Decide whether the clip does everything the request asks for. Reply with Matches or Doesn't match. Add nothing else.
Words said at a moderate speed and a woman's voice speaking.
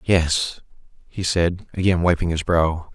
Doesn't match